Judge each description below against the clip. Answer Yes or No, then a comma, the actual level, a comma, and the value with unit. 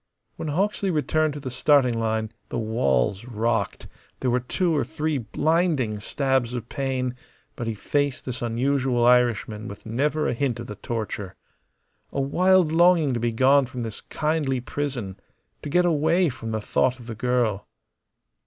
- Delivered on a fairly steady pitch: No, average, 4.3 semitones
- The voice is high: No, low, 125 Hz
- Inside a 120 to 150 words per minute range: No, average, 165 wpm